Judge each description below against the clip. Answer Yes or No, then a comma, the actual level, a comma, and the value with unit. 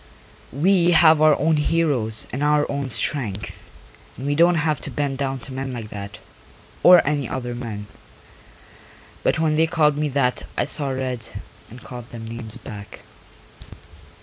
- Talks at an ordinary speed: Yes, average, 160 wpm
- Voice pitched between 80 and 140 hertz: Yes, low, 135 Hz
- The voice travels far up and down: No, average, 4.2 semitones